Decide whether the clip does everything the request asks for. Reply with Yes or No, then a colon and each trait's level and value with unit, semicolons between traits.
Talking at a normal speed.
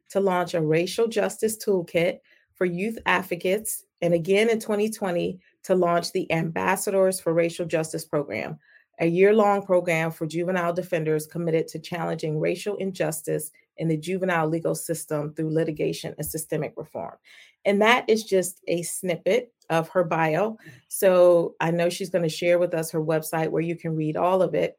Yes: average, 165 wpm